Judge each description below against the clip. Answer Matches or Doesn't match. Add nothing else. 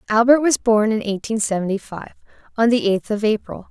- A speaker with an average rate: Matches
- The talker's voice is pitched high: Matches